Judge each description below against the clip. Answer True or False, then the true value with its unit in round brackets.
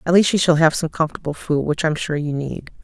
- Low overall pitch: False (160 Hz)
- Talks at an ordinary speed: False (275 wpm)